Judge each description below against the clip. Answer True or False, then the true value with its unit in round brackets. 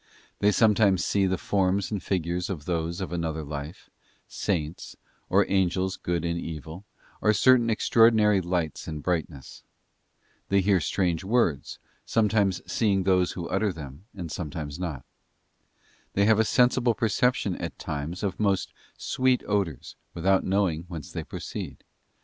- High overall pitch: False (95 Hz)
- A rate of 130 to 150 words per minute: True (145 wpm)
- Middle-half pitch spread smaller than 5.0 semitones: True (3.6 semitones)